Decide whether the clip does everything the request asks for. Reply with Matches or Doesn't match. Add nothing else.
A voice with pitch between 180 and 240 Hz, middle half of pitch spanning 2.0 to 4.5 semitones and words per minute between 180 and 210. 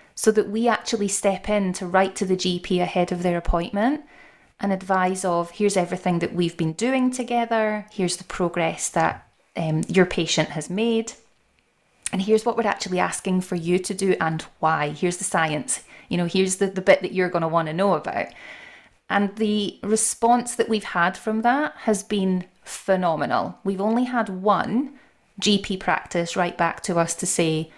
Matches